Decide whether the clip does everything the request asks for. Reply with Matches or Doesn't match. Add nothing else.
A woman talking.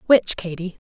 Matches